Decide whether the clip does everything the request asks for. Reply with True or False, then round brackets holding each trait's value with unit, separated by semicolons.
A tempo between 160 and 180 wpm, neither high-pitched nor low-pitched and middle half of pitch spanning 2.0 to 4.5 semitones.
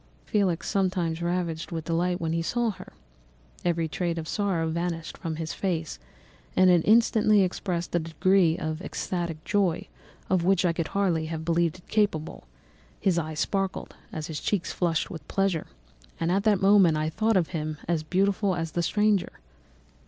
True (165 wpm; 175 Hz; 2.9 semitones)